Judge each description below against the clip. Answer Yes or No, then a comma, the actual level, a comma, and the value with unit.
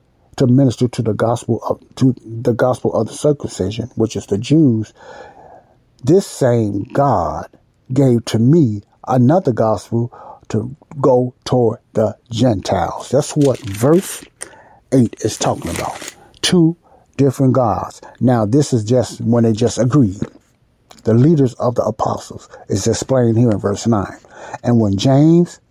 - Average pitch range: Yes, average, 3.0 semitones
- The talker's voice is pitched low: Yes, low, 120 Hz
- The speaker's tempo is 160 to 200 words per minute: No, average, 140 wpm